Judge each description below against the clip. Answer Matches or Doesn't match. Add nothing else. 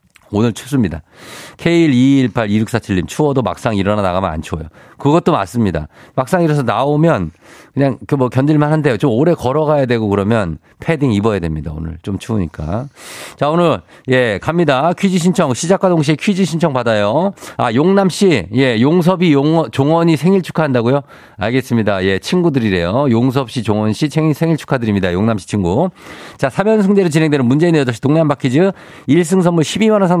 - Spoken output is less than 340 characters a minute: Doesn't match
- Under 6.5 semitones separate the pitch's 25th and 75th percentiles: Doesn't match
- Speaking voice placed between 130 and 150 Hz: Matches